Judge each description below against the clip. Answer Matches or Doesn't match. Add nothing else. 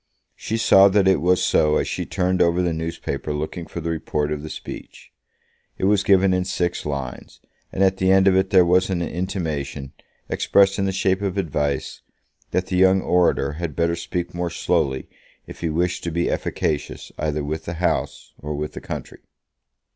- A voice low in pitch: Matches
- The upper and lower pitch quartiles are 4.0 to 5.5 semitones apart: Doesn't match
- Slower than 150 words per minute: Doesn't match